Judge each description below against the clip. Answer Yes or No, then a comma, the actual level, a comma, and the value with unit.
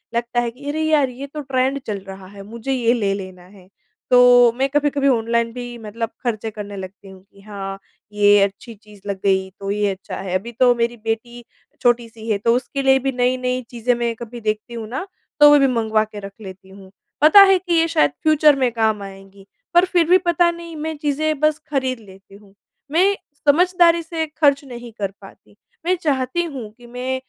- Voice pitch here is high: Yes, high, 240 Hz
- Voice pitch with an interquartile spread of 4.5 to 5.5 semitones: Yes, average, 5.2 semitones